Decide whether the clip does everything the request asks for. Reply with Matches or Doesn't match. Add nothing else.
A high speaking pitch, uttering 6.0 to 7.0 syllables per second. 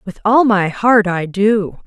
Doesn't match